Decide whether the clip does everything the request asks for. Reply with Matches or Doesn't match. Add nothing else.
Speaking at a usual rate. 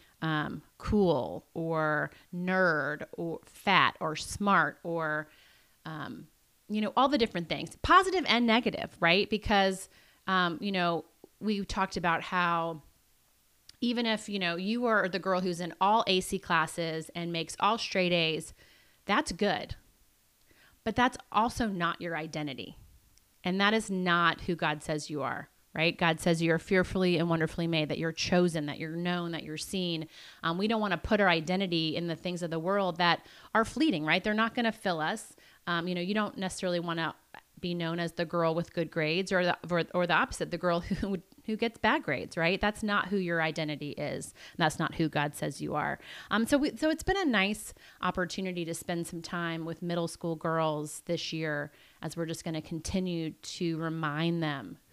Matches